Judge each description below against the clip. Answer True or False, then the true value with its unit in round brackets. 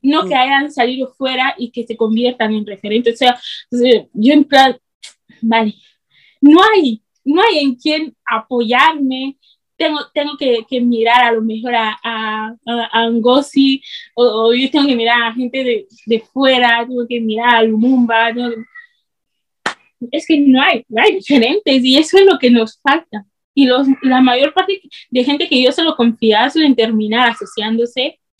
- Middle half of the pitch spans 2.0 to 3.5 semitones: True (3.2 semitones)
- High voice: True (250 Hz)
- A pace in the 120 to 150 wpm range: False (175 wpm)